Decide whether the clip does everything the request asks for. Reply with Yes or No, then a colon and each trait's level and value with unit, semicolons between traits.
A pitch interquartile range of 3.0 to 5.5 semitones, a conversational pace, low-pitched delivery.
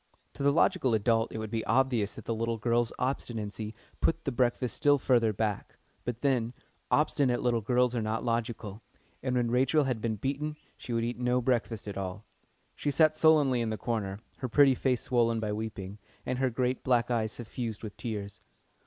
No: narrow, 2.6 semitones; average, 190 wpm; low, 120 Hz